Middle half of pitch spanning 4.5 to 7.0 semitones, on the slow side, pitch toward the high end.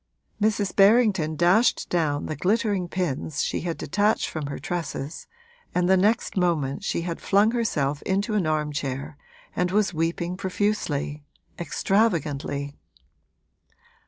No: average, 5.1 semitones; slow, 125 wpm; medium, 175 Hz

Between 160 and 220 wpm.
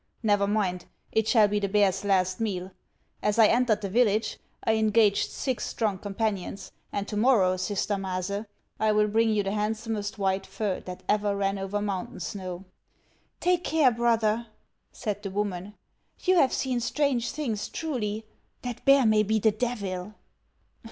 Yes: average, 165 wpm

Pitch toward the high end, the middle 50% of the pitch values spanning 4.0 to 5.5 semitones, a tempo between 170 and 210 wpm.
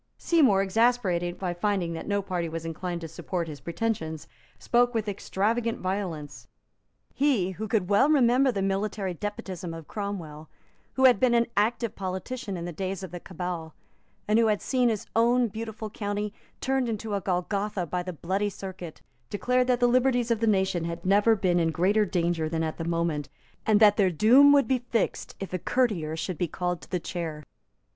Yes: high, 195 Hz; average, 4.6 semitones; average, 190 wpm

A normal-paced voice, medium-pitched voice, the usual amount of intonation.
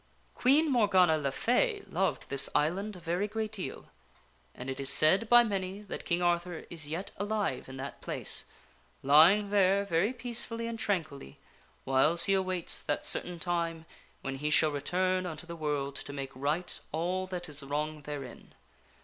Yes: average, 165 wpm; medium, 175 Hz; average, 5.0 semitones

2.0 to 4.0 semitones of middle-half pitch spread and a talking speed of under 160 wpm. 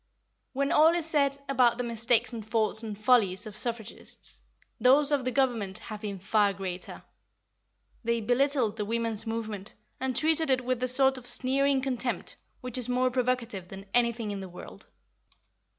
No: average, 3.3 semitones; average, 165 wpm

